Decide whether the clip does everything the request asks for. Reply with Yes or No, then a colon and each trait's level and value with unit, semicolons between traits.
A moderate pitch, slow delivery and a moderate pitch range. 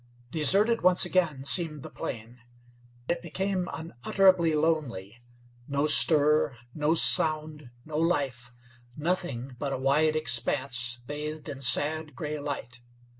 Yes: medium, 150 Hz; slow, 120 wpm; average, 3.5 semitones